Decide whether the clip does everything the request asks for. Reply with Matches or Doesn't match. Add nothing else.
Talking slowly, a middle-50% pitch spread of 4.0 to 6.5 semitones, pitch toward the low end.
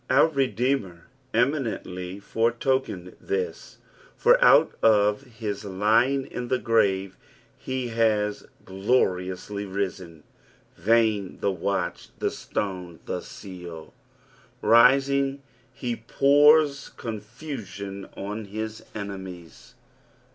Matches